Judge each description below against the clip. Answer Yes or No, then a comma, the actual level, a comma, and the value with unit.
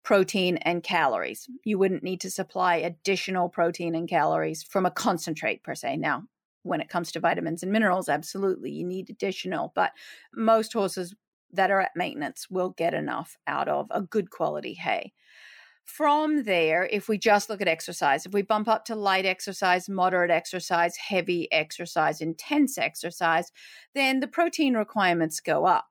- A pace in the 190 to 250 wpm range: No, average, 165 wpm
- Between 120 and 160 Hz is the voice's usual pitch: No, medium, 185 Hz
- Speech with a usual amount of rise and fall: Yes, average, 3.9 semitones